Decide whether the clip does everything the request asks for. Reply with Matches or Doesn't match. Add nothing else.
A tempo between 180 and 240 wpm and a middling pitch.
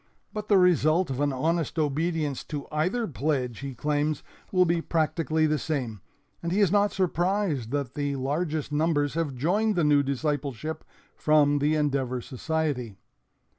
Doesn't match